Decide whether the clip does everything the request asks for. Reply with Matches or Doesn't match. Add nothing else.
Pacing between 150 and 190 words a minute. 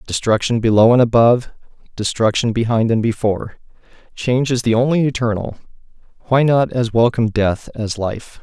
Doesn't match